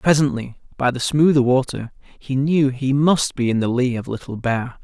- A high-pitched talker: No, low, 130 Hz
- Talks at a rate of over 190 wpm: Yes, average, 200 wpm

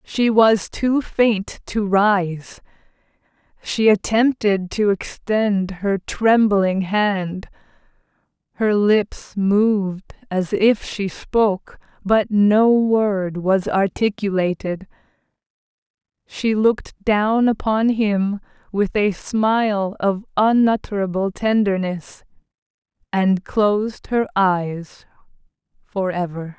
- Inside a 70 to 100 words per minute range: Yes, slow, 90 wpm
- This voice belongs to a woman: Yes, female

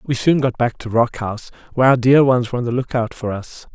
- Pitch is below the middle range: Yes, low, 125 Hz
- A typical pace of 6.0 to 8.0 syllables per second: Yes, 6.1 syllables/s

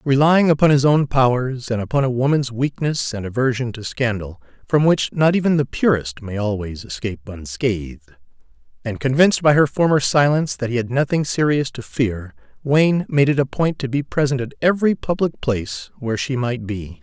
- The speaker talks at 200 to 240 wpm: No, average, 185 wpm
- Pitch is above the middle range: No, low, 130 Hz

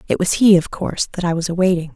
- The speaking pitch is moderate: Yes, medium, 175 Hz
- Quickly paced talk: Yes, fast, 275 wpm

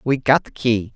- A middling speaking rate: No, fast, 250 wpm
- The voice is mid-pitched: No, low, 125 Hz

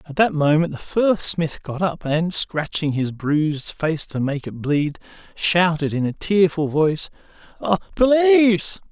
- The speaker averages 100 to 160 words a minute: Yes, average, 155 wpm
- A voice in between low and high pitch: Yes, medium, 170 Hz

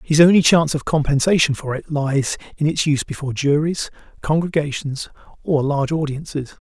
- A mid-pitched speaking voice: Yes, medium, 150 Hz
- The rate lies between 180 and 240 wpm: No, average, 155 wpm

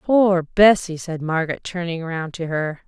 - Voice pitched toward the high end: No, medium, 170 Hz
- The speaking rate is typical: Yes, average, 165 wpm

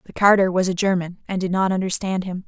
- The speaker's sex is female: Yes, female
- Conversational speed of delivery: No, fast, 240 wpm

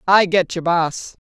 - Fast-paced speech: No, average, 190 wpm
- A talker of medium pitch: Yes, medium, 175 Hz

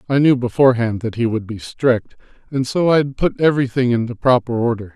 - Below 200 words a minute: No, fast, 205 wpm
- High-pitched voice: No, low, 125 Hz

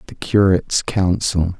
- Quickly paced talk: No, slow, 115 wpm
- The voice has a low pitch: Yes, very low, 95 Hz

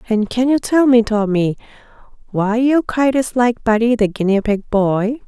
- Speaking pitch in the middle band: No, high, 230 Hz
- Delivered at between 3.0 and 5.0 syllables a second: Yes, 4.4 syllables/s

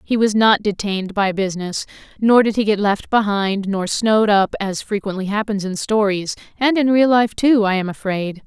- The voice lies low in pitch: No, high, 205 Hz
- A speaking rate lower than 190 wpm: No, average, 200 wpm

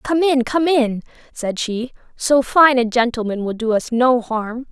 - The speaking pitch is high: Yes, high, 245 Hz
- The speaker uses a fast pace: No, average, 190 wpm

